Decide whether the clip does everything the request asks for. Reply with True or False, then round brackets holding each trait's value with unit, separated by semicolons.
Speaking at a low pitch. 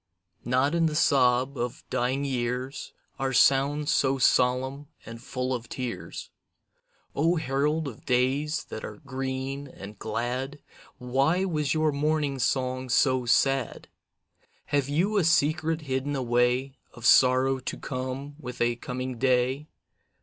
True (130 Hz)